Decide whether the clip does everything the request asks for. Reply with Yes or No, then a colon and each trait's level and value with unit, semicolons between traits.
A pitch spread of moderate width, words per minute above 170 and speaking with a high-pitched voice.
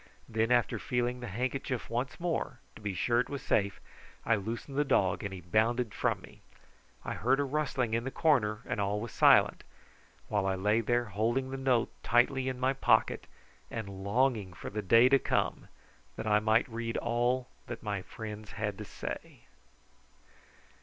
No: average, 3.4 semitones; average, 180 wpm; low, 115 Hz